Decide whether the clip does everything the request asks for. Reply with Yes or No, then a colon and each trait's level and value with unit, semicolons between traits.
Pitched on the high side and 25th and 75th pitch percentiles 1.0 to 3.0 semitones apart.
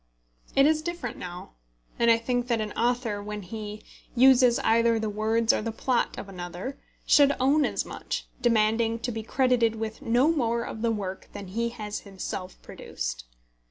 Yes: high, 230 Hz; average, 2.7 semitones